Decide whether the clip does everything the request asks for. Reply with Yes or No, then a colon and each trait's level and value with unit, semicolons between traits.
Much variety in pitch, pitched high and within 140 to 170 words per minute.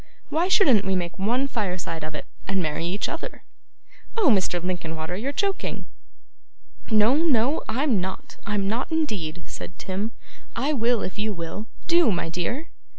Yes: wide, 7.1 semitones; high, 210 Hz; average, 155 wpm